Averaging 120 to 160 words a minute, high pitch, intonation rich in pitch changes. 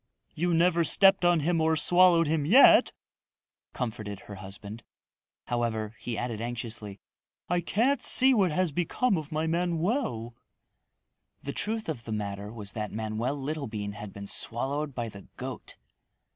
No: average, 145 wpm; medium, 140 Hz; wide, 7.9 semitones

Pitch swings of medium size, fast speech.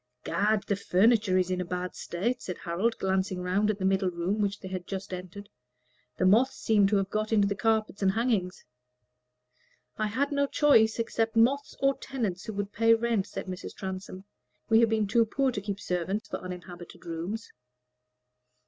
No: average, 3.3 semitones; average, 185 wpm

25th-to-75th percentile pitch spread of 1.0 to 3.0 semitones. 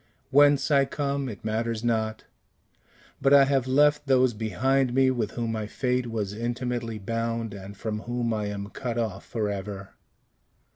No: average, 3.4 semitones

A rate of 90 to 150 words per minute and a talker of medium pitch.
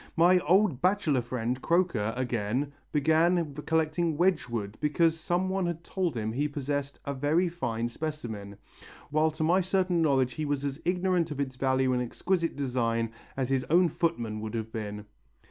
No: average, 165 wpm; medium, 145 Hz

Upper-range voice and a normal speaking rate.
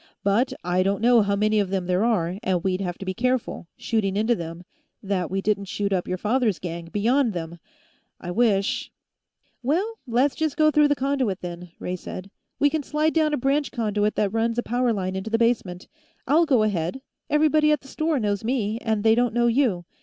No: high, 220 Hz; fast, 210 wpm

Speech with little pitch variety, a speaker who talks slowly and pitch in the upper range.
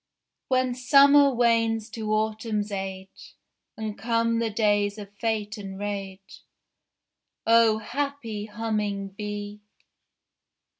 Yes: narrow, 2.0 semitones; slow, 100 wpm; high, 215 Hz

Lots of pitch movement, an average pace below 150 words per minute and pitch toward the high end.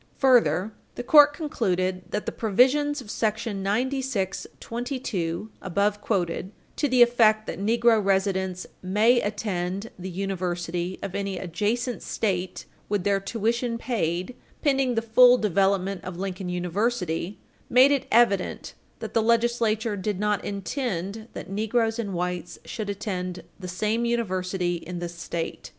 No: average, 4.2 semitones; slow, 135 wpm; high, 205 Hz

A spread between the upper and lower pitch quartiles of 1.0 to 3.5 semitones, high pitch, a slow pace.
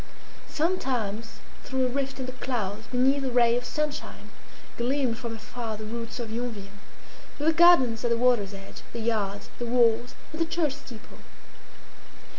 No: average, 2.9 semitones; high, 240 Hz; average, 165 wpm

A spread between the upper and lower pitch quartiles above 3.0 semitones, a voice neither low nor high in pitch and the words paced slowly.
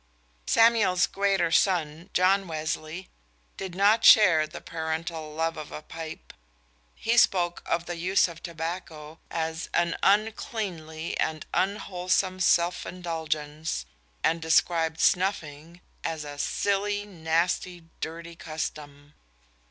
No: average, 2.7 semitones; medium, 170 Hz; slow, 115 wpm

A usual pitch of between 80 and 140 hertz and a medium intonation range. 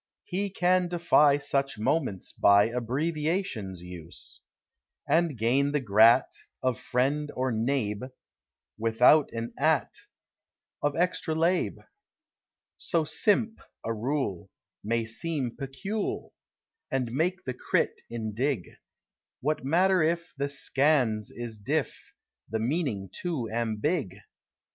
No: low, 135 Hz; wide, 6.0 semitones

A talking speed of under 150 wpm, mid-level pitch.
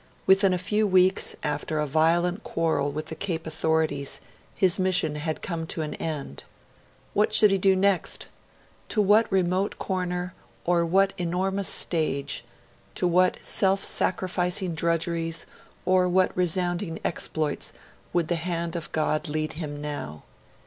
Yes: average, 140 wpm; medium, 175 Hz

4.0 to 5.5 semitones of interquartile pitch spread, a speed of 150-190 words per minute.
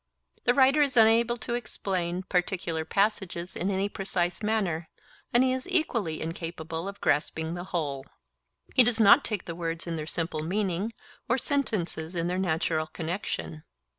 Yes: average, 5.1 semitones; average, 155 wpm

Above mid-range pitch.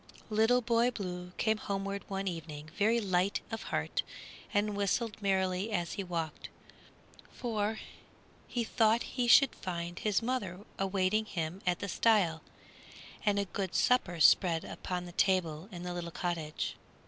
Yes: high, 195 Hz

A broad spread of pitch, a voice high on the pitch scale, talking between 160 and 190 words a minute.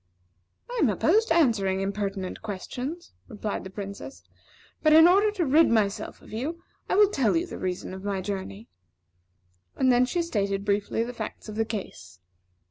Yes: wide, 8.3 semitones; high, 220 Hz; average, 175 wpm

